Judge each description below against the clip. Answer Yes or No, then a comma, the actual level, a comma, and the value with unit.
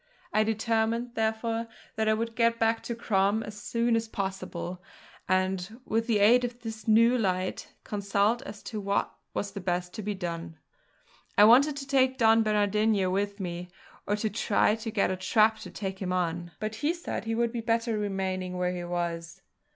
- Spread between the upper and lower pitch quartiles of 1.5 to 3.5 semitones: Yes, average, 3.2 semitones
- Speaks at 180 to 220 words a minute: Yes, average, 185 wpm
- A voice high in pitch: Yes, high, 215 Hz